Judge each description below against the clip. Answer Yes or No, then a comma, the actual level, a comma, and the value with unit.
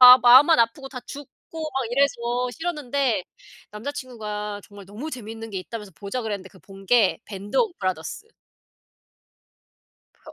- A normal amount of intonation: Yes, average, 4.6 semitones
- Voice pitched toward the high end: Yes, high, 235 Hz